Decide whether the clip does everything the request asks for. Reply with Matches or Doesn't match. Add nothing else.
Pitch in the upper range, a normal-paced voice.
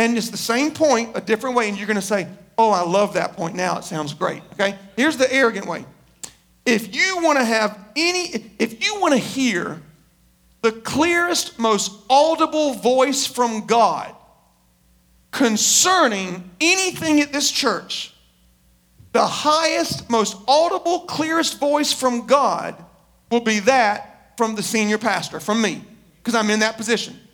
Matches